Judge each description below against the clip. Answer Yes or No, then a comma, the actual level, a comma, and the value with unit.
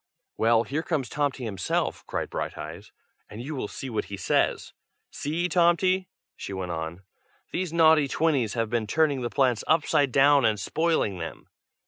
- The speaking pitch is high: No, low, 135 Hz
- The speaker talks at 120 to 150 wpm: No, average, 160 wpm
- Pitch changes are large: Yes, wide, 6.4 semitones